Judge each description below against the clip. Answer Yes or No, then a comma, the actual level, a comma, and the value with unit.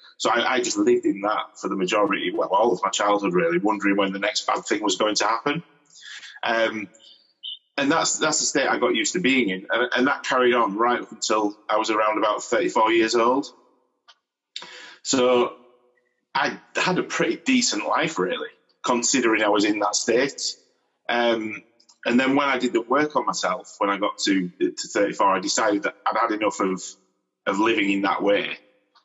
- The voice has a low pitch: Yes, low, 115 Hz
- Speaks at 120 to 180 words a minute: No, average, 195 wpm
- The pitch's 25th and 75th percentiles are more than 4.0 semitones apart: Yes, wide, 5.4 semitones